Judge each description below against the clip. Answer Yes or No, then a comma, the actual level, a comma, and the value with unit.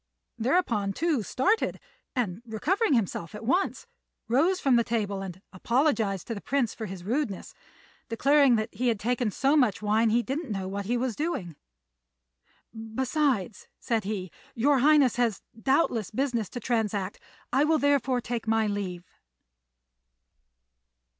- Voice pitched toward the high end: Yes, high, 235 Hz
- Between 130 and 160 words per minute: Yes, average, 145 wpm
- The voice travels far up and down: No, average, 4.7 semitones